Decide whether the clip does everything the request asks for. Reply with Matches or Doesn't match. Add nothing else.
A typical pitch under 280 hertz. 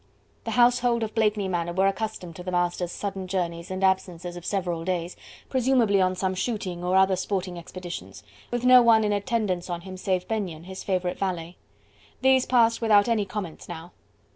Matches